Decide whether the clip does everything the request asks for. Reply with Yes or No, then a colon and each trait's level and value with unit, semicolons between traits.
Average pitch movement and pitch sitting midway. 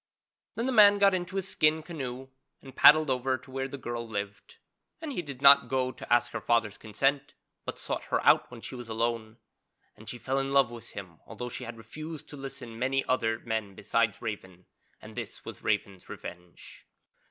No: average, 3.9 semitones; low, 125 Hz